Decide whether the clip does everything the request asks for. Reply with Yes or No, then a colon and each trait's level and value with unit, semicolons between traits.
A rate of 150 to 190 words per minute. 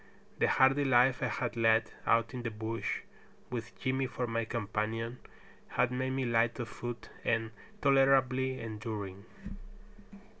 No: average, 140 wpm